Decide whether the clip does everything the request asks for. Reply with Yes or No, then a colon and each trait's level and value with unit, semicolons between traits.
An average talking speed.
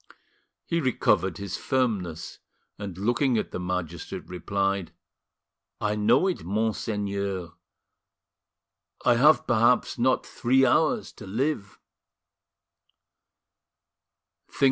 No: slow, 90 wpm